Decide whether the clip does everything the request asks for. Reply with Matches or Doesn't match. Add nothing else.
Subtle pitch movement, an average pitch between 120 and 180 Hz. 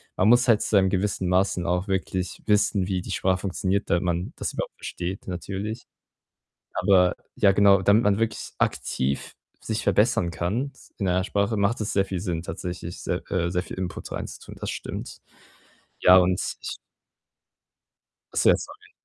Doesn't match